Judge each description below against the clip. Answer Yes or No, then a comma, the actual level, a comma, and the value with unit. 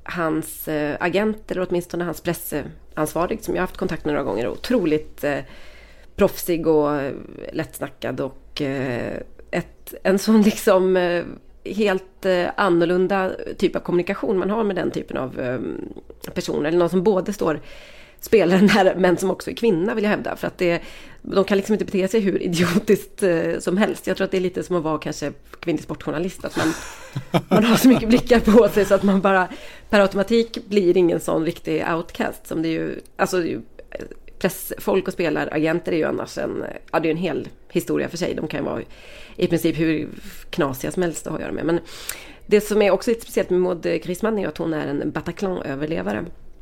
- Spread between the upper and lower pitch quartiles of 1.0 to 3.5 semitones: Yes, average, 3.2 semitones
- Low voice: No, medium, 180 Hz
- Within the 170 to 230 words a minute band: Yes, average, 190 wpm